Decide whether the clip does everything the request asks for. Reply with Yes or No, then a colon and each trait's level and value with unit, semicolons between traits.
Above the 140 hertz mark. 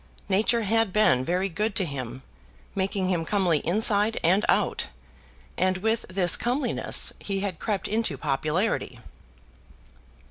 Yes: high, 190 Hz